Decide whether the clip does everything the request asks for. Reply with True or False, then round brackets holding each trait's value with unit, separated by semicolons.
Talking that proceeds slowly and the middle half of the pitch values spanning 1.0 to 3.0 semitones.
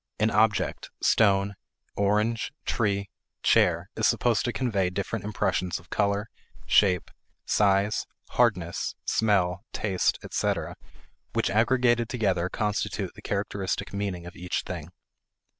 True (115 wpm; 2.4 semitones)